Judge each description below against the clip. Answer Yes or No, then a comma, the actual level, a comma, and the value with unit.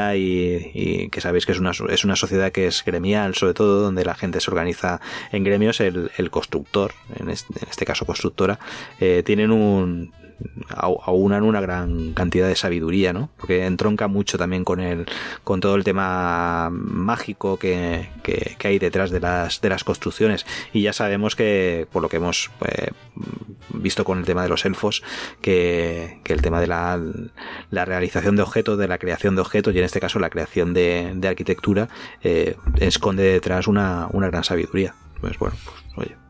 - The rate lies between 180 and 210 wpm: Yes, average, 185 wpm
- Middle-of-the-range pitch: No, very low, 90 Hz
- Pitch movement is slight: Yes, narrow, 2.2 semitones